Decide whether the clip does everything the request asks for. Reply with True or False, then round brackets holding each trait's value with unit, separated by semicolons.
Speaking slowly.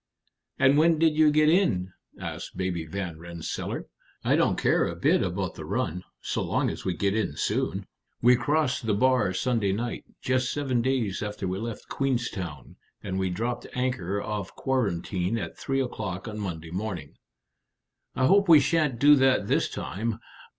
False (170 wpm)